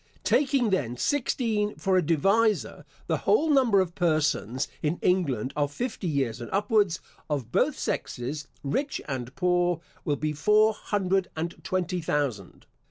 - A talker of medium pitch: Yes, medium, 175 Hz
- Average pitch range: No, wide, 6.3 semitones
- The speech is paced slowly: No, average, 145 wpm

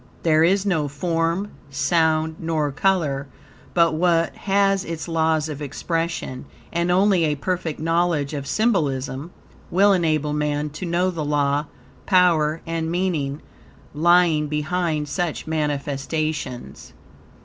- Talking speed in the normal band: No, slow, 120 wpm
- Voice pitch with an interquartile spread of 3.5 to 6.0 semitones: No, average, 2.9 semitones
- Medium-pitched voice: Yes, medium, 160 Hz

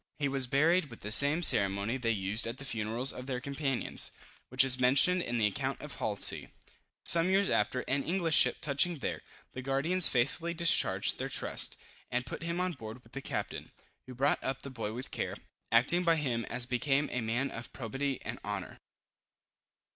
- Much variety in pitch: No, average, 4.1 semitones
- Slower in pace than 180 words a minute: No, average, 190 wpm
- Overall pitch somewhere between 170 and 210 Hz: No, low, 135 Hz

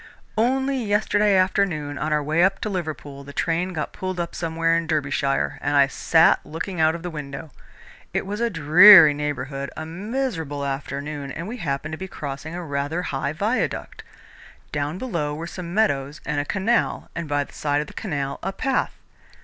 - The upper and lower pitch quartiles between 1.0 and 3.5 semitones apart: No, average, 4.7 semitones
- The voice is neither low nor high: Yes, medium, 160 Hz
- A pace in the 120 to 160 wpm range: No, average, 185 wpm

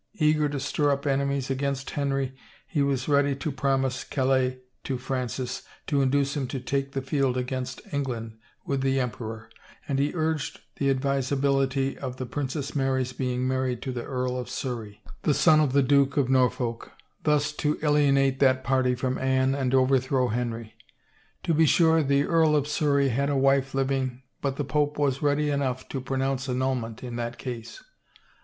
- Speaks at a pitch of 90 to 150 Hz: Yes, low, 135 Hz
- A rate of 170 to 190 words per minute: Yes, average, 175 wpm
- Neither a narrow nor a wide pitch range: No, narrow, 1.6 semitones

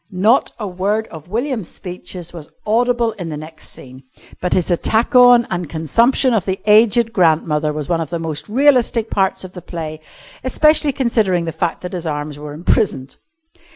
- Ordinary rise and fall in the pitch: No, wide, 6.2 semitones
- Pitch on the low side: No, medium, 185 Hz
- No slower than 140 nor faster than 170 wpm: No, average, 180 wpm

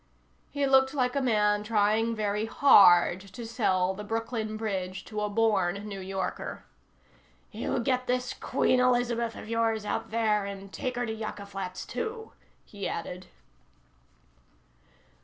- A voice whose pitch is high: Yes, high, 215 Hz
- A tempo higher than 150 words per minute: No, average, 145 wpm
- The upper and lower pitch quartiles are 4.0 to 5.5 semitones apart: No, average, 3.2 semitones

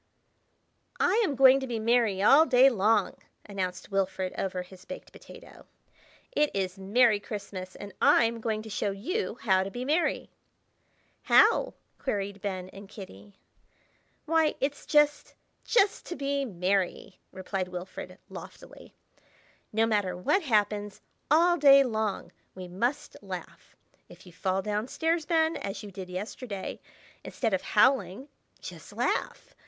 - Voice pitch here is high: Yes, high, 210 Hz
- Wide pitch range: Yes, wide, 6.1 semitones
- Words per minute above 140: No, slow, 135 wpm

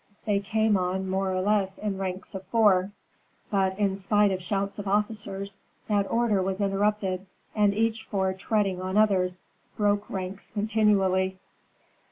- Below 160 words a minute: Yes, average, 150 wpm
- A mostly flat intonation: Yes, narrow, 1.7 semitones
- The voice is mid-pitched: No, high, 195 Hz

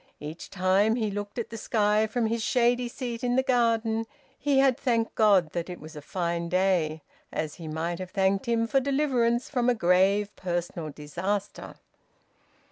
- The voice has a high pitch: Yes, high, 210 Hz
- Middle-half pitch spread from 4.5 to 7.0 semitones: Yes, average, 5.1 semitones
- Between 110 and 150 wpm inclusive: No, average, 175 wpm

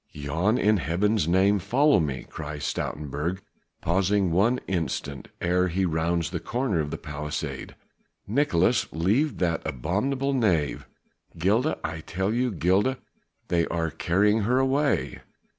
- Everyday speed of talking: No, slow, 130 wpm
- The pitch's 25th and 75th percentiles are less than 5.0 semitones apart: No, average, 5.3 semitones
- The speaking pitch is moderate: No, very low, 90 Hz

